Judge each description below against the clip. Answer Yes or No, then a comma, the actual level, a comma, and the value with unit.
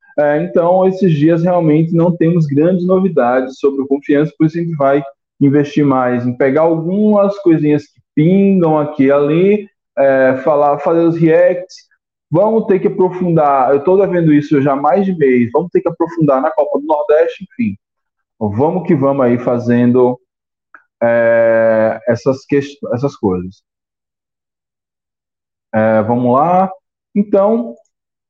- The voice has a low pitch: No, medium, 150 Hz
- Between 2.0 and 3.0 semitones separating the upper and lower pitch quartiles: No, average, 5.0 semitones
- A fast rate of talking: No, average, 150 wpm